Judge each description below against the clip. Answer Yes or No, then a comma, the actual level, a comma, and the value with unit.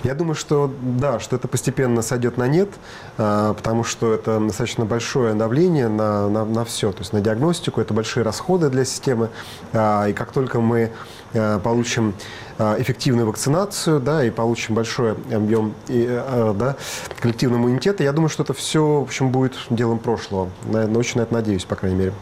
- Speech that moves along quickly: Yes, fast, 165 wpm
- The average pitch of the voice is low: Yes, low, 115 Hz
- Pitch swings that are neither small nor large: Yes, average, 3.1 semitones